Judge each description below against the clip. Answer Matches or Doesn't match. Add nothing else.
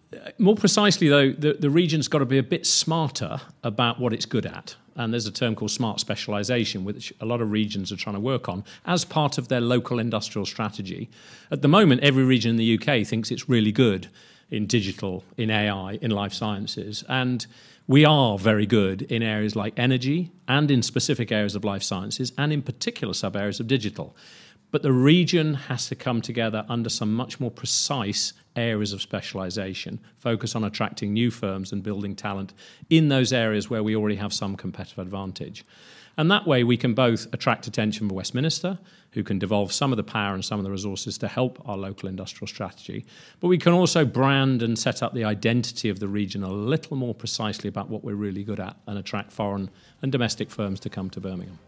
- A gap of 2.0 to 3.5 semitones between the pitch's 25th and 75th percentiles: Doesn't match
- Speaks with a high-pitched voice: Doesn't match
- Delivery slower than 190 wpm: Doesn't match